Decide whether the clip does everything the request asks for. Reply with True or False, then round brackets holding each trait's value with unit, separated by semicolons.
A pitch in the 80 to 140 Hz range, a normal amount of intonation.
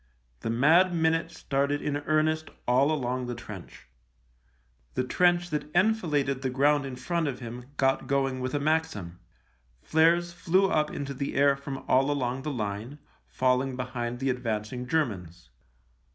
True (135 Hz; 3.9 semitones)